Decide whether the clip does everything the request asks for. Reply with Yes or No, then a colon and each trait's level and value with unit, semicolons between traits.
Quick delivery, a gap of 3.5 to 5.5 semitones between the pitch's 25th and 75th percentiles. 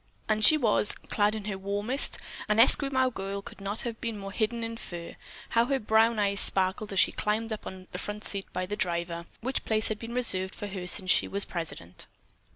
No: fast, 215 wpm; average, 2.9 semitones